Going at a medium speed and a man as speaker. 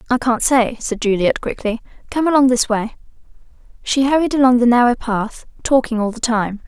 No: average, 180 wpm; female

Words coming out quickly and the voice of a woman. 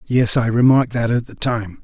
No: fast, 230 wpm; male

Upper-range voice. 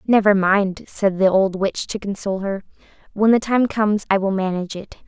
Yes: high, 200 Hz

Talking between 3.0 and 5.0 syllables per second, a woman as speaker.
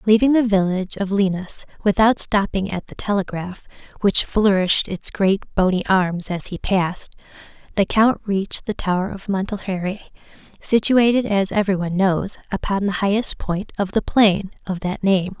Yes: 4.8 syllables/s; female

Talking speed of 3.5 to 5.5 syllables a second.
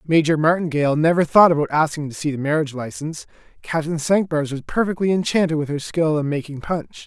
No: 6.1 syllables/s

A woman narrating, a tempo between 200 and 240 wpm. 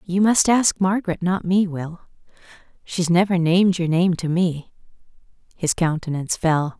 No: female; average, 150 wpm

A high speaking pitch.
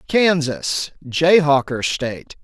No: medium, 155 Hz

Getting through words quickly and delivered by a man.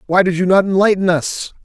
Yes: fast, 220 wpm; male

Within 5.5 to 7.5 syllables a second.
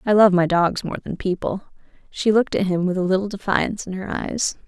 Yes: 5.8 syllables/s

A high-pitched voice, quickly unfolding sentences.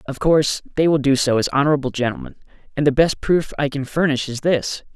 No: medium, 145 Hz; fast, 220 wpm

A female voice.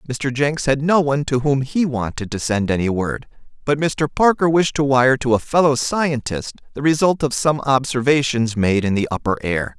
No: male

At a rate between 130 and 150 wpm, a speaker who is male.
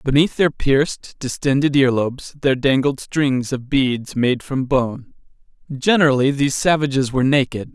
Yes: average, 140 wpm; male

